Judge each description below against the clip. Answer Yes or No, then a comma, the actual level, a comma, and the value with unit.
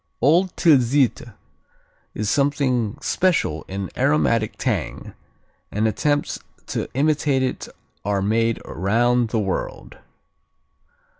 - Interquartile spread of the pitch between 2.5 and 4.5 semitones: No, average, 4.9 semitones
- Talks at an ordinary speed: No, slow, 95 wpm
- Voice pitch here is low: Yes, low, 120 Hz